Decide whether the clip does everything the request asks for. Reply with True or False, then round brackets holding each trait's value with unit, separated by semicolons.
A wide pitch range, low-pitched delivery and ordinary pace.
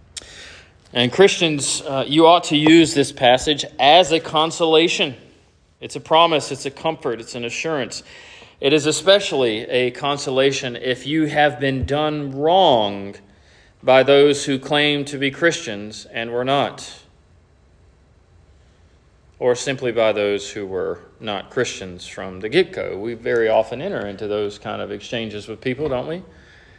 True (6.5 semitones; 130 Hz; 150 wpm)